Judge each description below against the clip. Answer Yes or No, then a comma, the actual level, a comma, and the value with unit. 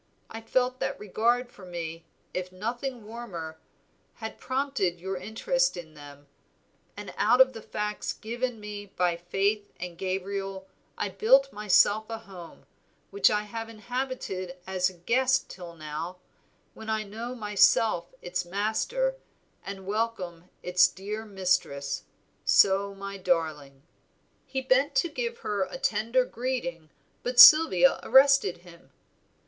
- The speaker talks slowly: Yes, slow, 130 wpm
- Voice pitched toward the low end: No, high, 205 Hz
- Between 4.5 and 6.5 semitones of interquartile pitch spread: Yes, average, 5.1 semitones